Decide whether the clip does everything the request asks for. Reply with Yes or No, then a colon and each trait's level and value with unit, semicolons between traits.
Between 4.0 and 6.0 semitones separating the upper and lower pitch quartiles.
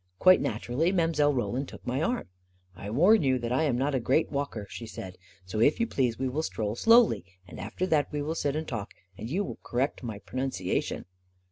Yes: wide, 5.4 semitones